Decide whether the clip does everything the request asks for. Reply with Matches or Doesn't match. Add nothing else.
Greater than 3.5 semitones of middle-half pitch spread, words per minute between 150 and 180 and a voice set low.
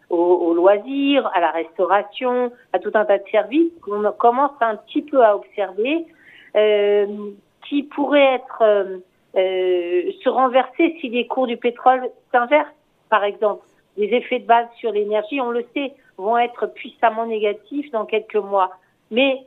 Doesn't match